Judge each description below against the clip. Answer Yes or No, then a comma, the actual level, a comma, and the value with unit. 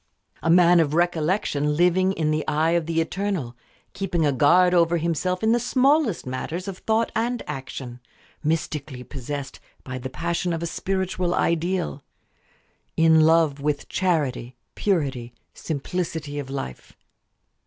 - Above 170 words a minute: No, average, 140 wpm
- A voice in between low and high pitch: Yes, medium, 165 Hz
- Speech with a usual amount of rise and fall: Yes, average, 4.0 semitones